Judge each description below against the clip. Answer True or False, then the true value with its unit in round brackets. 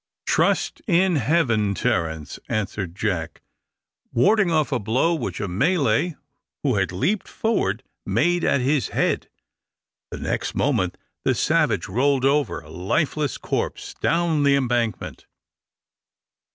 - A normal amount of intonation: False (7.8 semitones)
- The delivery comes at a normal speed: False (125 wpm)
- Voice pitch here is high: False (130 Hz)